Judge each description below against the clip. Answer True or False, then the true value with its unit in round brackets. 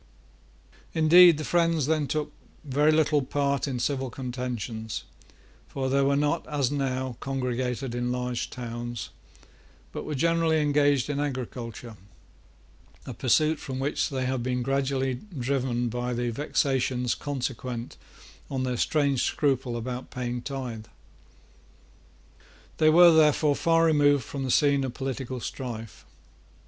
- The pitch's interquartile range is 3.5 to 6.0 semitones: False (2.9 semitones)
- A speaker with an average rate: False (130 wpm)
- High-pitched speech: False (135 Hz)